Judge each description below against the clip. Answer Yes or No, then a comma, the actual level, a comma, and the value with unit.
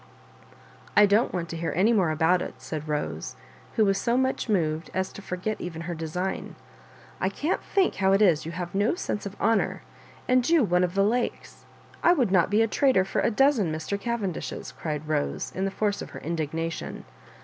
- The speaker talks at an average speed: No, fast, 215 wpm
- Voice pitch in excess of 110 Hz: Yes, high, 190 Hz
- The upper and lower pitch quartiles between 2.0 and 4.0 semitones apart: No, average, 4.7 semitones